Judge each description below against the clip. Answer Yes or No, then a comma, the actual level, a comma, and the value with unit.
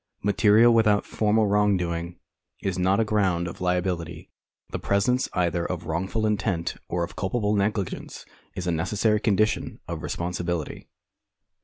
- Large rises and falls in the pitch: No, average, 3.3 semitones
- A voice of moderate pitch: No, very low, 95 Hz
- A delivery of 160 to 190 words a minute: No, slow, 135 wpm